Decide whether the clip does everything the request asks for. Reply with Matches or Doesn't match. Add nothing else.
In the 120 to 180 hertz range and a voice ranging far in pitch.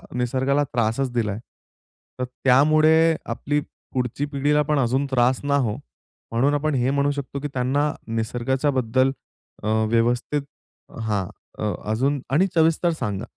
Doesn't match